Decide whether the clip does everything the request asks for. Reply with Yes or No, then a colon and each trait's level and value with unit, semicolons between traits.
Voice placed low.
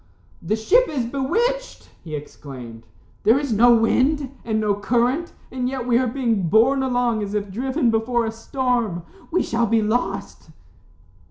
No: high, 235 Hz